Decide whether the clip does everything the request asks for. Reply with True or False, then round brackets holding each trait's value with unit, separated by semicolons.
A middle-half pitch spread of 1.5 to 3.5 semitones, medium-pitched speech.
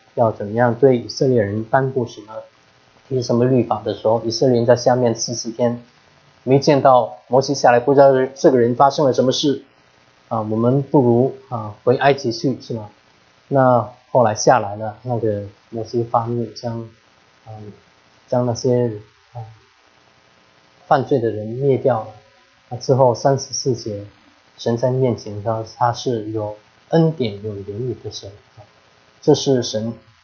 False (3.2 semitones; 115 Hz)